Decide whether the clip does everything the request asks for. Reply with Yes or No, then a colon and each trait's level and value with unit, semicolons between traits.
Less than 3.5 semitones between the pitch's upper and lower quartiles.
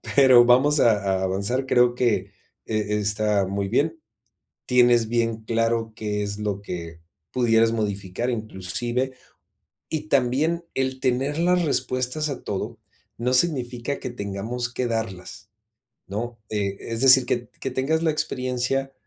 No: average, 3.8 semitones